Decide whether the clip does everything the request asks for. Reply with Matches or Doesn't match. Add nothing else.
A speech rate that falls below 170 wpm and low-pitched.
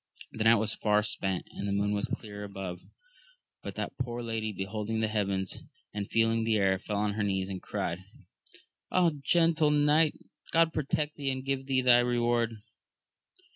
Doesn't match